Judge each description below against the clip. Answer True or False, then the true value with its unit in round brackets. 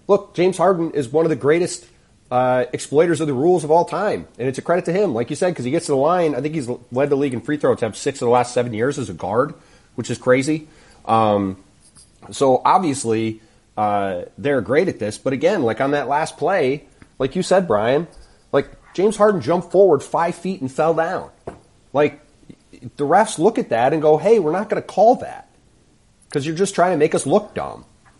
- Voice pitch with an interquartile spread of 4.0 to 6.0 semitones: True (5.5 semitones)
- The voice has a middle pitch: True (150 Hz)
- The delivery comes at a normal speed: False (225 wpm)